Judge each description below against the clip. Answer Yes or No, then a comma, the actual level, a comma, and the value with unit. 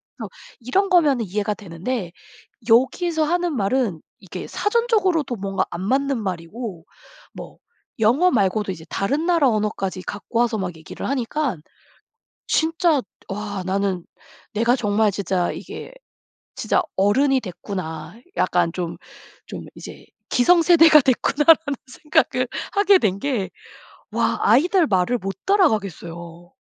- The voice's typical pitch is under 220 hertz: No, high, 225 Hz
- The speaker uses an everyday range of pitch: No, wide, 7.9 semitones